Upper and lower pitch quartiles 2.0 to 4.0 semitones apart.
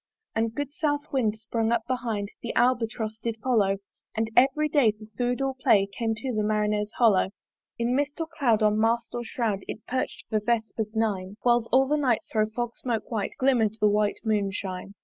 Yes: average, 2.8 semitones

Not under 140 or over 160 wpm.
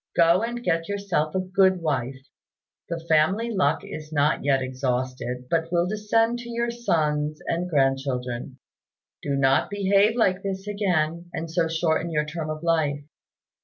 Yes: average, 155 wpm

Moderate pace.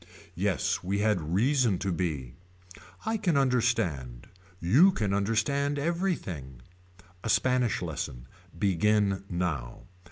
No: slow, 105 wpm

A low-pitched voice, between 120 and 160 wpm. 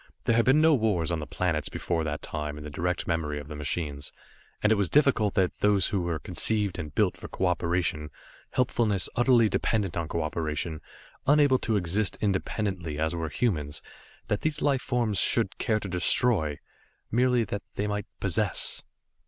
No: very low, 95 Hz; average, 175 wpm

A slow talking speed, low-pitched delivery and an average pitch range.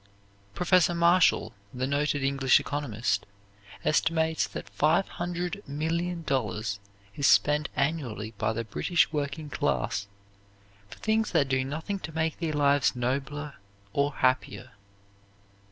No: slow, 110 wpm; medium, 145 Hz; average, 3.9 semitones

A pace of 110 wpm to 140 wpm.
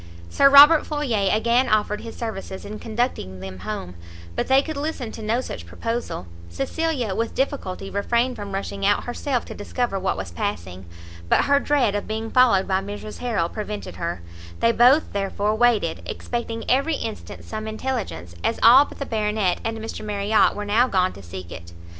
No: average, 180 wpm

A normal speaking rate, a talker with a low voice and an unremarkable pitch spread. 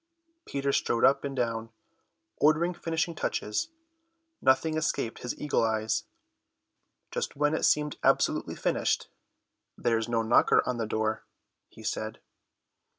No: slow, 125 wpm; low, 125 Hz; average, 4.9 semitones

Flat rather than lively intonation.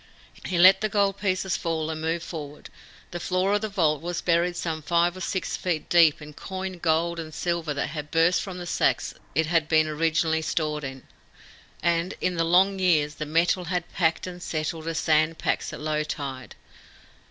Yes: narrow, 2.3 semitones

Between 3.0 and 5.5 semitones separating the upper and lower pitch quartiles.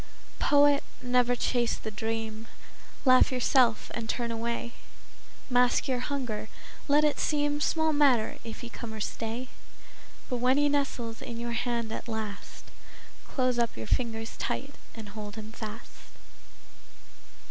No: narrow, 2.5 semitones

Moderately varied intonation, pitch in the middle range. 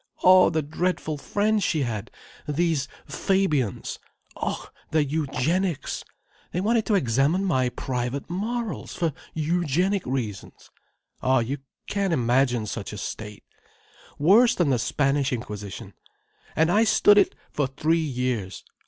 No: wide, 6.3 semitones; medium, 150 Hz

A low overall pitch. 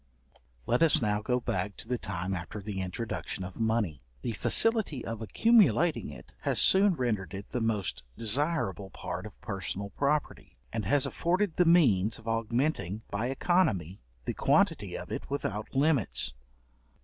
Yes: low, 115 Hz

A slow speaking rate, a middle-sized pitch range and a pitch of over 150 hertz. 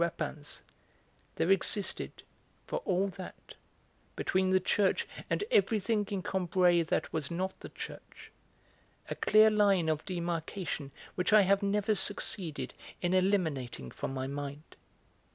Yes: slow, 130 wpm; average, 3.7 semitones; medium, 185 Hz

